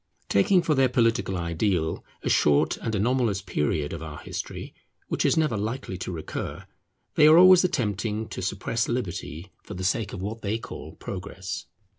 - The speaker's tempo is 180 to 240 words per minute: No, average, 170 wpm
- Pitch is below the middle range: Yes, low, 105 Hz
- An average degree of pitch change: Yes, average, 4.8 semitones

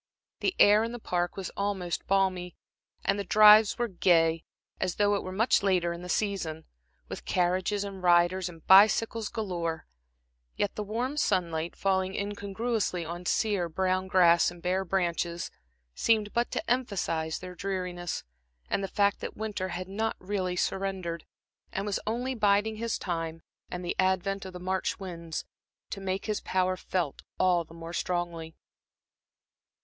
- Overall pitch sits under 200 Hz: Yes, medium, 185 Hz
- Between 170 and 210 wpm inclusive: No, average, 160 wpm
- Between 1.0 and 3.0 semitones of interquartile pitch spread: Yes, average, 2.7 semitones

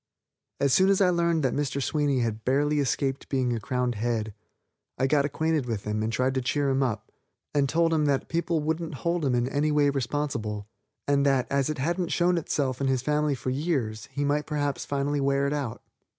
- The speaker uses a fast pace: Yes, fast, 215 wpm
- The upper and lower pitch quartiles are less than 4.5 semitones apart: Yes, average, 2.9 semitones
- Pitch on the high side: No, medium, 140 Hz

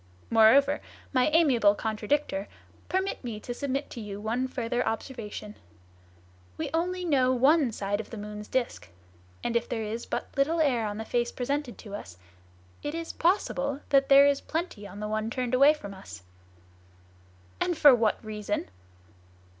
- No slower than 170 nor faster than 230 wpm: No, average, 160 wpm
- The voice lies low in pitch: No, high, 245 Hz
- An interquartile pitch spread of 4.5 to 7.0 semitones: Yes, average, 4.8 semitones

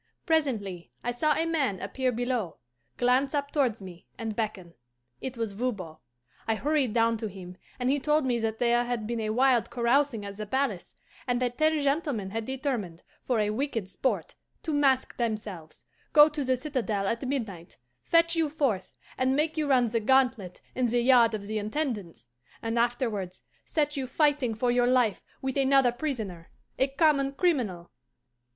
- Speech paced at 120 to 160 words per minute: No, average, 175 wpm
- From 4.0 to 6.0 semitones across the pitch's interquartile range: Yes, average, 4.3 semitones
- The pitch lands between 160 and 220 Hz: No, high, 245 Hz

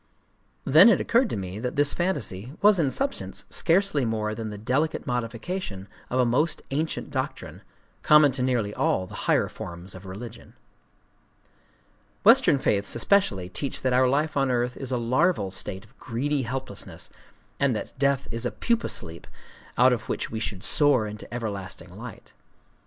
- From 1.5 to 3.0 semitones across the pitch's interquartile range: No, average, 5.3 semitones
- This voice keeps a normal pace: Yes, average, 165 wpm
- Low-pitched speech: Yes, low, 125 Hz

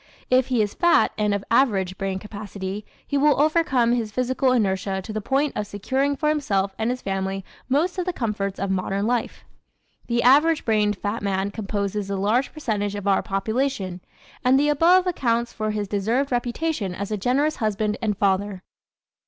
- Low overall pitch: No, high, 215 Hz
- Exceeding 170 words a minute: Yes, average, 180 wpm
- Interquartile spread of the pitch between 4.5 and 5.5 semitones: Yes, average, 4.9 semitones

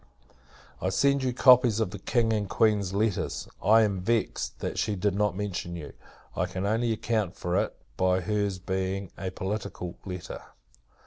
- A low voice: Yes, low, 100 Hz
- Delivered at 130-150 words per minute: No, average, 170 wpm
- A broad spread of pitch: No, average, 3.0 semitones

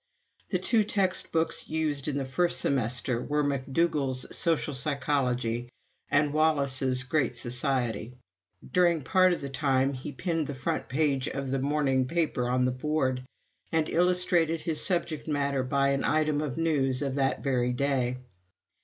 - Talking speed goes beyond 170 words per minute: No, average, 150 wpm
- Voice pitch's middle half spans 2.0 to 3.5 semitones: Yes, average, 3.2 semitones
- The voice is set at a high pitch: No, medium, 140 Hz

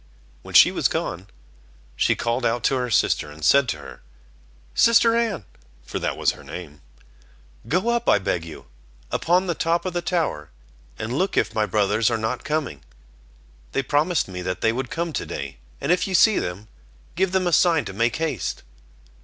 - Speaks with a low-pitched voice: Yes, low, 125 Hz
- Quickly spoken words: No, average, 190 wpm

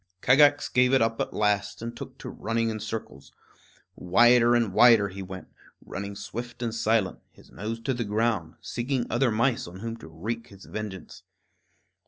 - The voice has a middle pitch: No, low, 115 Hz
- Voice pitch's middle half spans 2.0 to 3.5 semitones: Yes, average, 2.9 semitones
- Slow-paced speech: No, average, 175 wpm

